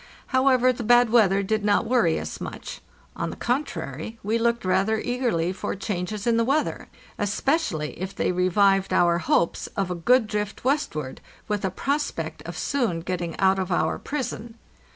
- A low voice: No, high, 205 Hz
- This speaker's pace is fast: No, average, 170 wpm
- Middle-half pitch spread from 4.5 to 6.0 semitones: Yes, average, 4.9 semitones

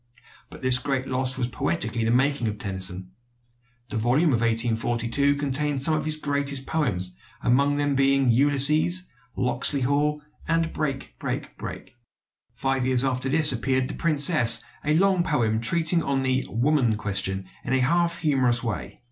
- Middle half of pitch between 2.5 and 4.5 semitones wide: Yes, average, 3.7 semitones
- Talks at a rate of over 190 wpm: No, average, 155 wpm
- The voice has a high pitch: No, low, 135 Hz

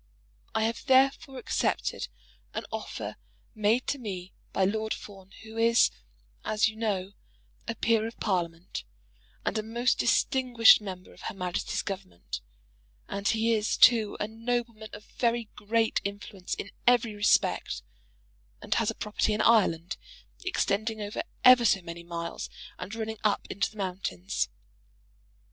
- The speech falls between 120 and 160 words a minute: Yes, average, 145 wpm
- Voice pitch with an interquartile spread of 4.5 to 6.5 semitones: No, average, 2.9 semitones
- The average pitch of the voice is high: Yes, high, 215 Hz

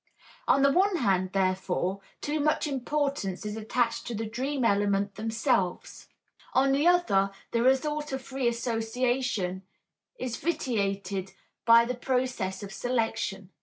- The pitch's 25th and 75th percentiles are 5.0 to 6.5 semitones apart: Yes, average, 5.3 semitones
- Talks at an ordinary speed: No, slow, 130 wpm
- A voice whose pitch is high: Yes, high, 235 Hz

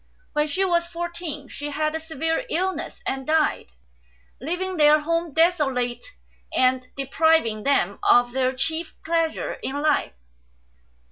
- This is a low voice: No, very high, 310 Hz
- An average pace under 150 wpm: Yes, slow, 135 wpm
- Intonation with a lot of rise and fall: No, average, 3.8 semitones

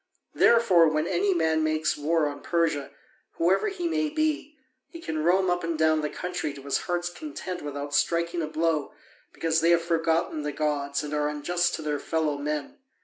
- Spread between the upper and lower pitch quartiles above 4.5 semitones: No, average, 2.8 semitones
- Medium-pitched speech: Yes, medium, 165 Hz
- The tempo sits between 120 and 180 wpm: No, average, 190 wpm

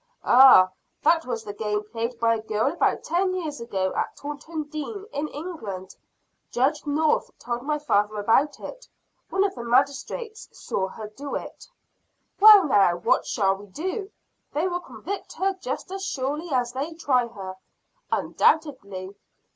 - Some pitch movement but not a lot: No, wide, 7.1 semitones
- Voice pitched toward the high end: Yes, very high, 275 Hz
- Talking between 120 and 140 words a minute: No, average, 155 wpm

